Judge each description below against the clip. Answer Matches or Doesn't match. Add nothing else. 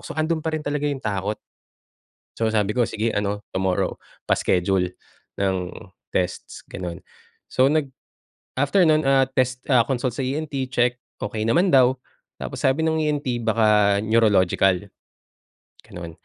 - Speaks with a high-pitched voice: Doesn't match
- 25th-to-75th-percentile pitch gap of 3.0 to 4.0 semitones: Doesn't match